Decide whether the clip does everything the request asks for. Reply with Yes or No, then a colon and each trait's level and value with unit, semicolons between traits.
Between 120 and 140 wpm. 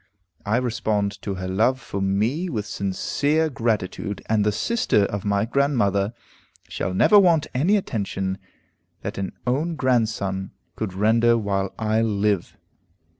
Yes: slow, 135 wpm